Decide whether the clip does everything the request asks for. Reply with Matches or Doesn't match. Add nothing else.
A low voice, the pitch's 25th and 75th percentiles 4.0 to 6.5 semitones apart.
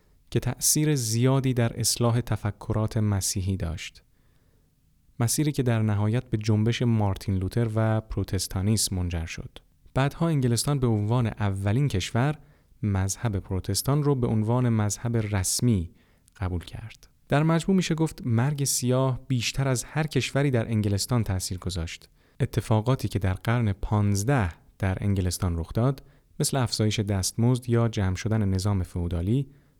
Matches